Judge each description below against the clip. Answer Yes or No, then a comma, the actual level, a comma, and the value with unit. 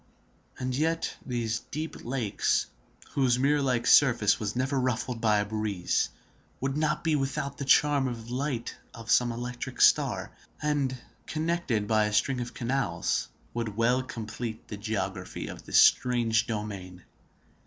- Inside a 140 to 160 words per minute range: Yes, average, 145 wpm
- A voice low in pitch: Yes, low, 120 Hz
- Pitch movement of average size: Yes, average, 3.8 semitones